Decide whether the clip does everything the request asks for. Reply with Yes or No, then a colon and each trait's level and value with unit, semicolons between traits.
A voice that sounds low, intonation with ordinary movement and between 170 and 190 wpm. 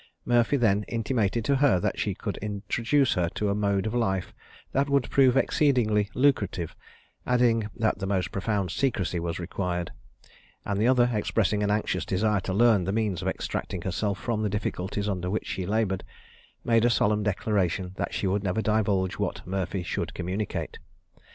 Yes: low, 105 Hz; average, 3.4 semitones; average, 175 wpm